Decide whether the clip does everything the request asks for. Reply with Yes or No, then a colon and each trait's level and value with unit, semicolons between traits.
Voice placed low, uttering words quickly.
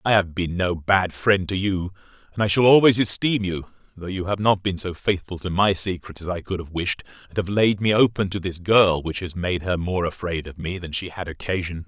Yes: very low, 95 Hz; fast, 250 wpm